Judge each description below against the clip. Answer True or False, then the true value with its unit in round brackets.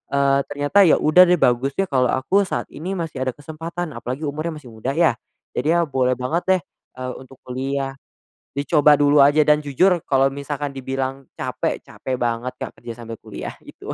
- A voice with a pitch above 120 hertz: True (140 Hz)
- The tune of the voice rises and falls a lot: False (3.1 semitones)